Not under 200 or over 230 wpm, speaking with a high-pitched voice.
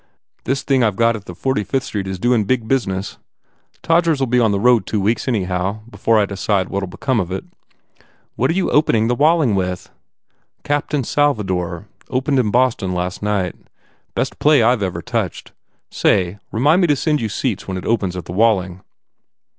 No: fast, 205 wpm; low, 110 Hz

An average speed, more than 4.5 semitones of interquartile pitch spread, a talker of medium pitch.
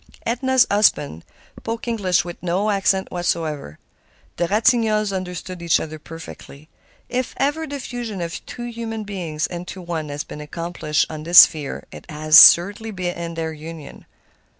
Yes: average, 150 wpm; wide, 5.4 semitones; medium, 175 Hz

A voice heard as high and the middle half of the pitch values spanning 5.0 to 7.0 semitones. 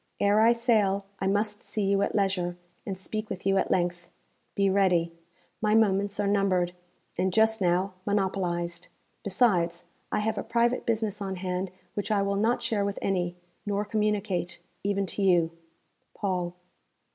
No: high, 195 Hz; narrow, 2.5 semitones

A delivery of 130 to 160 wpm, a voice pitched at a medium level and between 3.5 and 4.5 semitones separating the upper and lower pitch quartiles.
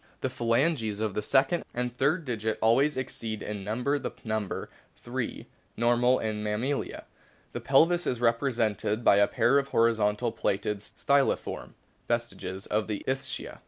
No: average, 150 wpm; low, 115 Hz; average, 3.9 semitones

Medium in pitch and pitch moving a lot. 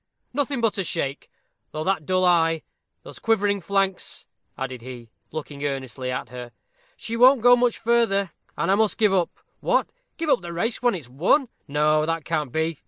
Yes: medium, 175 Hz; wide, 7.1 semitones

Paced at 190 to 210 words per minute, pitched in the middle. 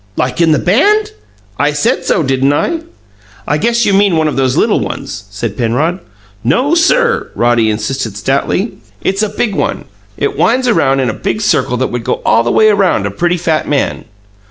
Yes: average, 195 wpm; medium, 155 Hz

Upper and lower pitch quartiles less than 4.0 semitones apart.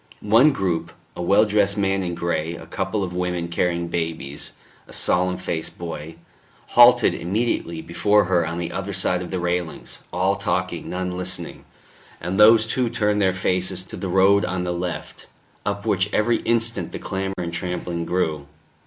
Yes: narrow, 2.6 semitones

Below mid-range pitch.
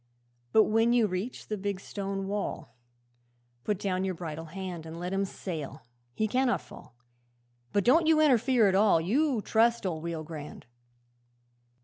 No: high, 195 Hz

